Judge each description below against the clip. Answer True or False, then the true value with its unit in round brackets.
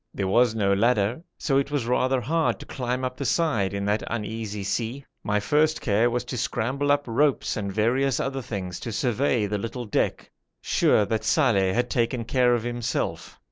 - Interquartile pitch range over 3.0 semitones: True (3.8 semitones)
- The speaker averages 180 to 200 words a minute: True (190 wpm)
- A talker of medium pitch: False (120 Hz)